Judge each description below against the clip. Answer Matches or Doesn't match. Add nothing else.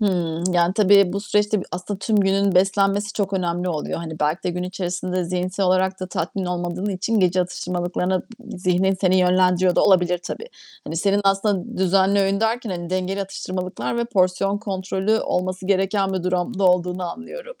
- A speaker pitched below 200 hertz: Matches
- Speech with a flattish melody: Matches